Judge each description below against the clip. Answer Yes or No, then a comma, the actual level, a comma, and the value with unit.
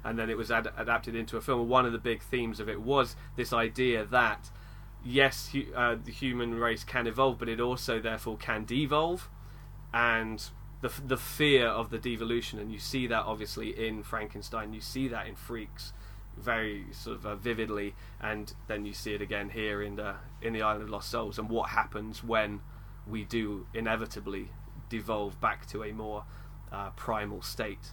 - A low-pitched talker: Yes, low, 115 Hz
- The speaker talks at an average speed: Yes, average, 190 wpm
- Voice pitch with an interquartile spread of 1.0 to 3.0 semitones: Yes, narrow, 2.4 semitones